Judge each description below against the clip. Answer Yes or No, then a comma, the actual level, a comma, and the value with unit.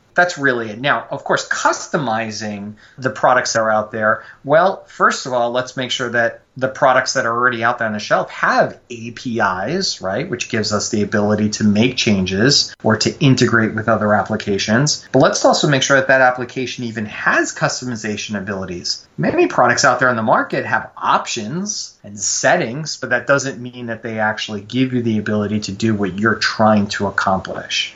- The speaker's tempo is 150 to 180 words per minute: No, average, 190 wpm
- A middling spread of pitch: Yes, average, 3.3 semitones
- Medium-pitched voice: No, low, 115 Hz